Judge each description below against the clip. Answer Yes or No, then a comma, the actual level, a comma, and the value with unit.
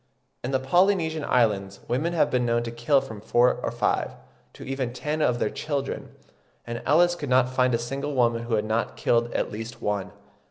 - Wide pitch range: No, average, 3.3 semitones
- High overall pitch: No, low, 125 Hz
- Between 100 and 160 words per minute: No, average, 200 wpm